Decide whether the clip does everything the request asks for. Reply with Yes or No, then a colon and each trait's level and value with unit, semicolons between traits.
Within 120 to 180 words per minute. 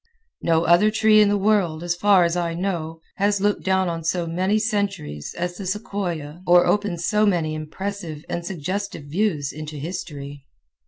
Yes: average, 170 wpm